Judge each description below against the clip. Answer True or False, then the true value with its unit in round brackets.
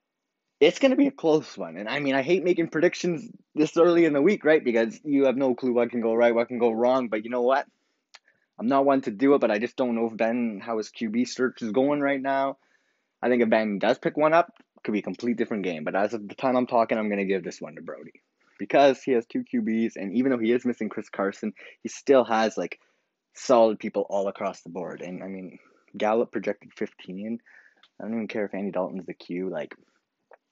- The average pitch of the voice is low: True (120 Hz)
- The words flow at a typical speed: False (245 wpm)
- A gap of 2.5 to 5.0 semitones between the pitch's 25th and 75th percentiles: True (4.4 semitones)